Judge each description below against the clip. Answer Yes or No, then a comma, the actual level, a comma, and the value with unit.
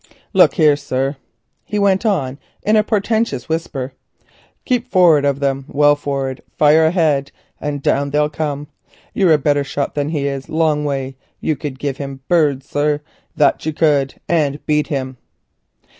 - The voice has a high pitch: No, medium, 145 Hz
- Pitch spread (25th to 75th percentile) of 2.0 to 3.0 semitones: Yes, narrow, 2.4 semitones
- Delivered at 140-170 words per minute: No, average, 180 wpm